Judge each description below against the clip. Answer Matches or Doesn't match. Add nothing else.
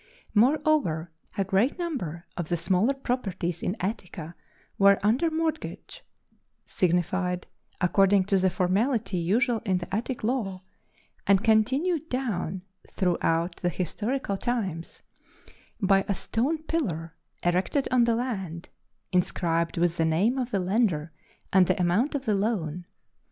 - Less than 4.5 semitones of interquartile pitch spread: Doesn't match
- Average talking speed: Doesn't match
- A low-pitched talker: Doesn't match